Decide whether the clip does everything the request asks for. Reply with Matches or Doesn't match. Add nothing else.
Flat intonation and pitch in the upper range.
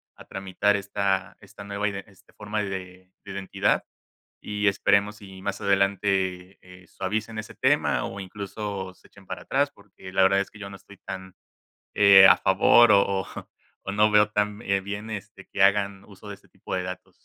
Doesn't match